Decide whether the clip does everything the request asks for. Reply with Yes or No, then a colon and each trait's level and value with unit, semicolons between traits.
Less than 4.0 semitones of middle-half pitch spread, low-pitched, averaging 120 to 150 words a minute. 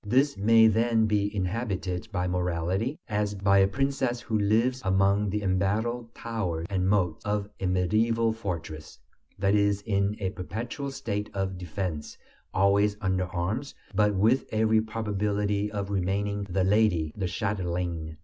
Yes: average, 2.8 semitones; low, 100 Hz; average, 145 wpm